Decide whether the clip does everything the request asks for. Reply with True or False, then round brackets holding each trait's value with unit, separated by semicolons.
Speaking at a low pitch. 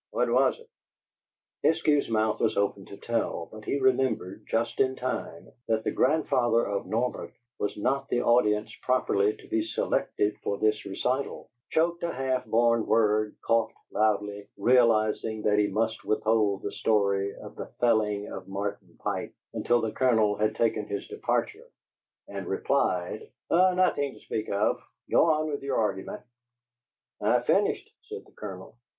True (110 Hz)